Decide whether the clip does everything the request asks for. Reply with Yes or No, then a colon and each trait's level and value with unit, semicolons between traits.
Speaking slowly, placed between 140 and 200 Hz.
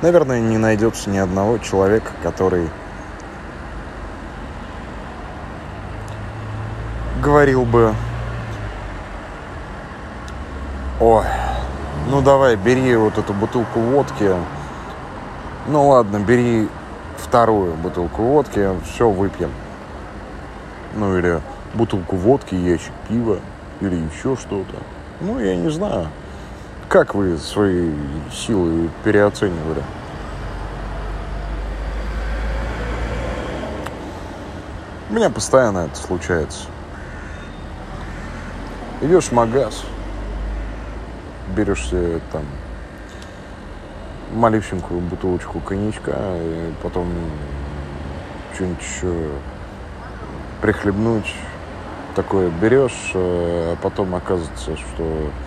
No: slow, 75 wpm; very low, 90 Hz